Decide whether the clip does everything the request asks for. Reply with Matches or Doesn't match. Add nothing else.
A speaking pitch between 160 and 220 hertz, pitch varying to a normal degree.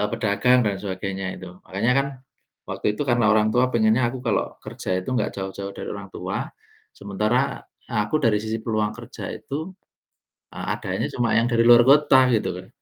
Doesn't match